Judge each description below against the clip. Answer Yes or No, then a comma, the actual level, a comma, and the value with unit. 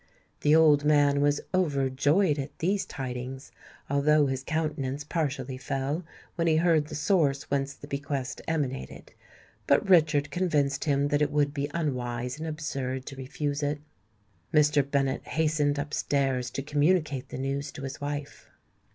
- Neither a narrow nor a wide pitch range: No, narrow, 1.9 semitones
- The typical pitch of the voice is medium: Yes, medium, 145 Hz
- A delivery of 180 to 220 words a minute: No, average, 150 wpm